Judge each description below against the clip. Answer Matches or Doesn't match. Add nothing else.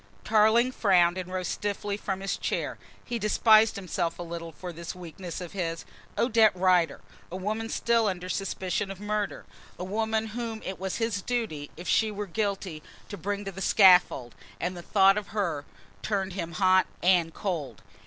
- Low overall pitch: Doesn't match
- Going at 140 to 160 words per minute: Doesn't match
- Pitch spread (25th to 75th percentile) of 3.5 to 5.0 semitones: Doesn't match